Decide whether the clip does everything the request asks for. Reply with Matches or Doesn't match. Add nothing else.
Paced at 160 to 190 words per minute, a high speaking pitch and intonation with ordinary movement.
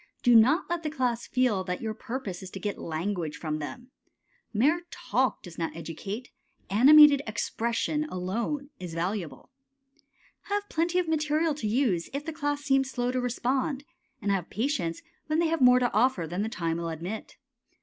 Doesn't match